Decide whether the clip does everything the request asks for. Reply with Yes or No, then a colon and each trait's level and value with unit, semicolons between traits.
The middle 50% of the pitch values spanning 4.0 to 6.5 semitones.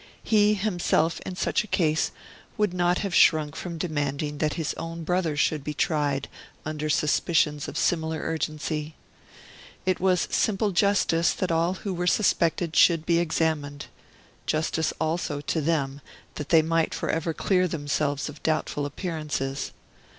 No: average, 2.7 semitones